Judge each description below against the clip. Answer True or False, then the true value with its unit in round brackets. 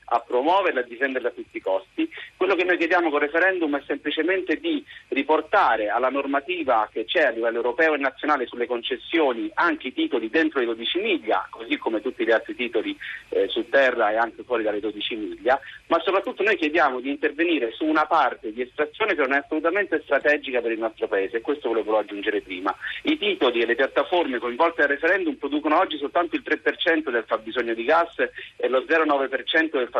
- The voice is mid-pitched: True (155 Hz)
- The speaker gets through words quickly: True (200 wpm)